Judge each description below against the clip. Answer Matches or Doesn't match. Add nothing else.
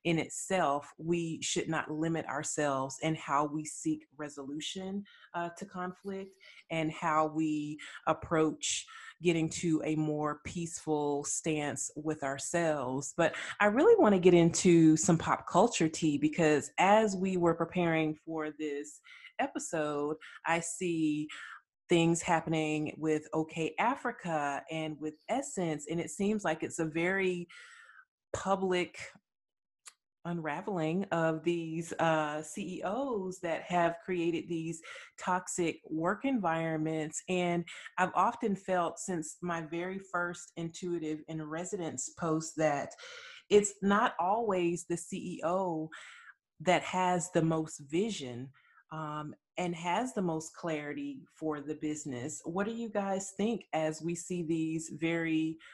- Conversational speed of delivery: Doesn't match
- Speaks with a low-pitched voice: Doesn't match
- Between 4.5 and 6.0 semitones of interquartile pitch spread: Doesn't match